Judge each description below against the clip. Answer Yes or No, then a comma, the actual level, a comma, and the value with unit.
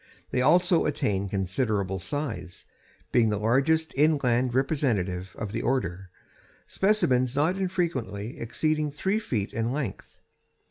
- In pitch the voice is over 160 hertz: No, low, 125 Hz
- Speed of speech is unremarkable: No, slow, 120 wpm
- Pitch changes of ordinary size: No, wide, 6.8 semitones